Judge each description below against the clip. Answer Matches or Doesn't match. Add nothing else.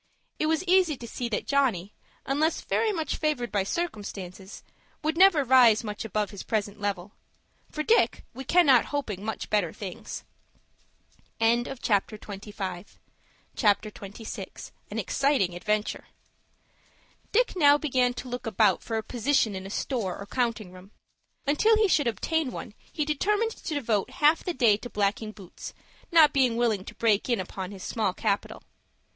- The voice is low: Doesn't match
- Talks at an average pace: Matches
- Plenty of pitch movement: Matches